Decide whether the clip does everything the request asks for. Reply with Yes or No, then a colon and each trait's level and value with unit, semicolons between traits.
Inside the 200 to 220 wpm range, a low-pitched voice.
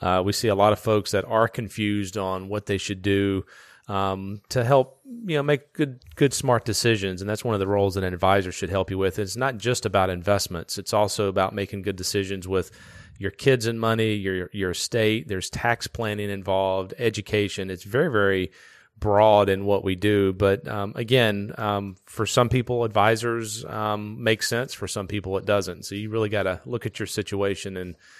Yes: fast, 205 wpm; low, 105 Hz